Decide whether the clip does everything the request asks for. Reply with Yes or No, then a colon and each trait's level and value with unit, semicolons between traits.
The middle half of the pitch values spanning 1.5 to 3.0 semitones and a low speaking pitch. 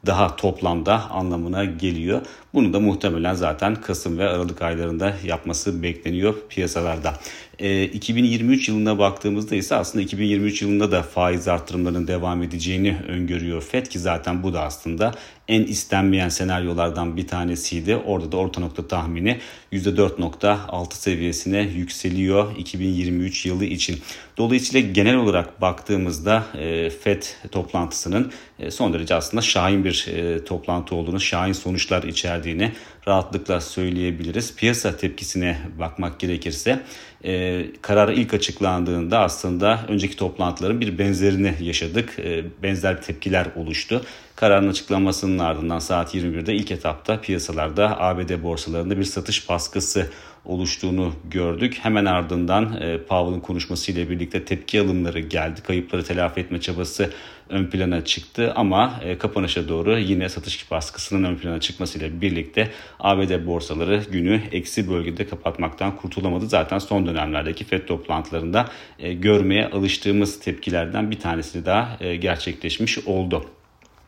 Yes: average, 2.7 semitones; very low, 90 Hz